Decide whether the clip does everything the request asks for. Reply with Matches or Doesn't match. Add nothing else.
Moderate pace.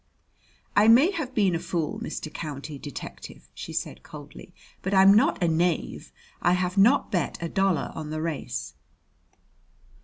Matches